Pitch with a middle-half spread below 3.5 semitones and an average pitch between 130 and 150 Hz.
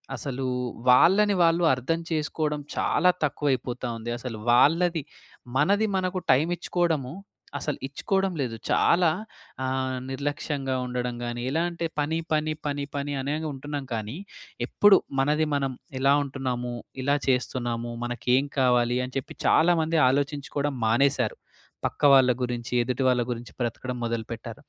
No: average, 3.8 semitones; low, 135 Hz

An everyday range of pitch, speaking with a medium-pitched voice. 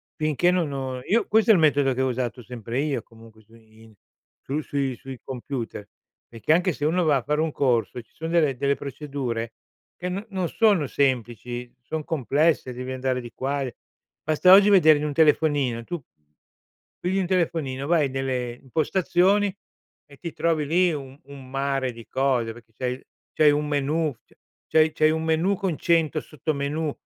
Yes: average, 4.1 semitones; medium, 145 Hz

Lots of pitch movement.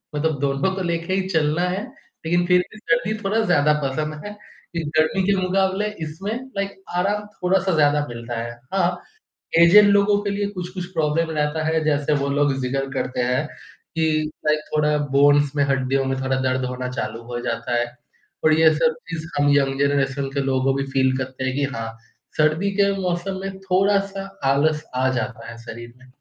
Yes: wide, 5.7 semitones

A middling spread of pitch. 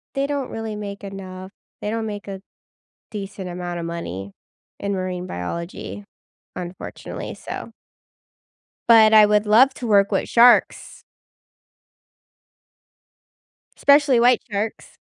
Yes: average, 3.3 semitones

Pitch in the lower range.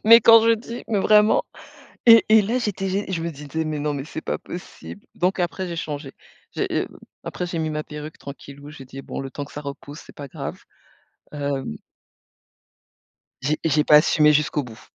No: medium, 155 Hz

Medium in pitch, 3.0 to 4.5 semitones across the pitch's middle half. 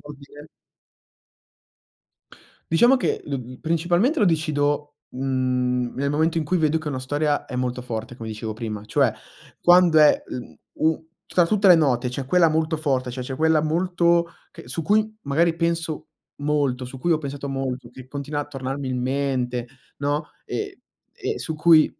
Yes: medium, 145 Hz; average, 4.1 semitones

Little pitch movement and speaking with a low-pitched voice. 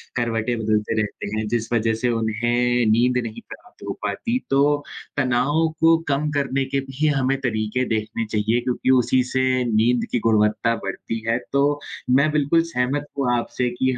No: average, 3.4 semitones; low, 120 Hz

